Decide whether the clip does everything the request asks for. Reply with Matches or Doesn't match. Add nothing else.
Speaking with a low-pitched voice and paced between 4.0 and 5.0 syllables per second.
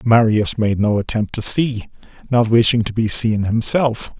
Matches